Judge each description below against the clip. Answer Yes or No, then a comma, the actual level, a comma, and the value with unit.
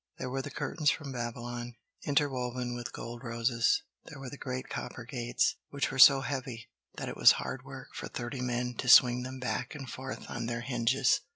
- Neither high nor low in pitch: No, low, 125 Hz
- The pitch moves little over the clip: Yes, narrow, 1.9 semitones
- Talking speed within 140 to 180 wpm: No, average, 195 wpm